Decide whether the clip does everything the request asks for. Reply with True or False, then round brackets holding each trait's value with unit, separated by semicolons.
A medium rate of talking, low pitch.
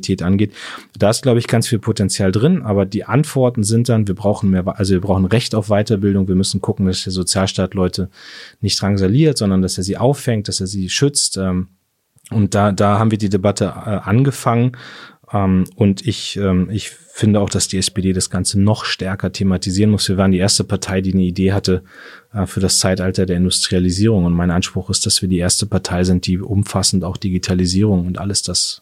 False (195 wpm; 100 Hz)